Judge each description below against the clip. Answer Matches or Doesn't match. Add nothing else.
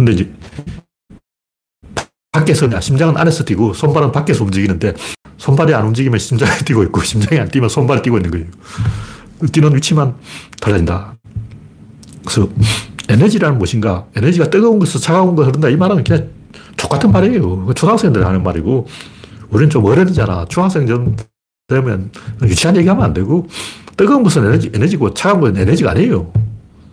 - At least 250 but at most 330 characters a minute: Doesn't match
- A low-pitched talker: Matches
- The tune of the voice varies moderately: Doesn't match